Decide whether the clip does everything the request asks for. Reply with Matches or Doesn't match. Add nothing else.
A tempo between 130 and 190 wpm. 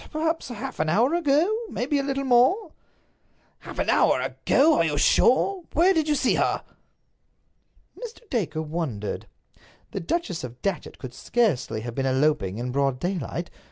Matches